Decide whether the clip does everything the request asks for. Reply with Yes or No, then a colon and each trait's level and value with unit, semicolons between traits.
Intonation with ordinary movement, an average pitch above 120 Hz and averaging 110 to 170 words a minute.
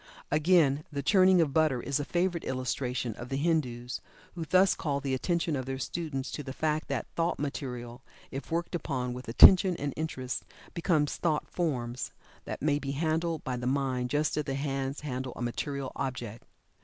No: average, 3.7 semitones; medium, 140 Hz; average, 180 wpm